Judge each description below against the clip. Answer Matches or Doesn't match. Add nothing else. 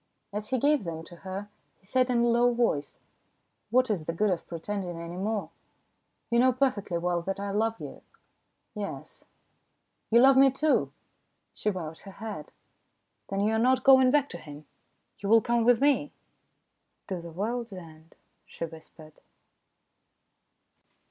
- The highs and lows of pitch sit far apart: Matches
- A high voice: Matches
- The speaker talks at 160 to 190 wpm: Matches